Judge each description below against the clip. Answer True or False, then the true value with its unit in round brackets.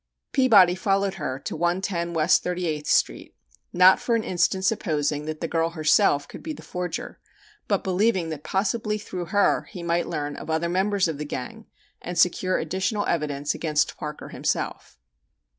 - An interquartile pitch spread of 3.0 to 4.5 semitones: True (3.6 semitones)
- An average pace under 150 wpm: False (170 wpm)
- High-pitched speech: False (175 Hz)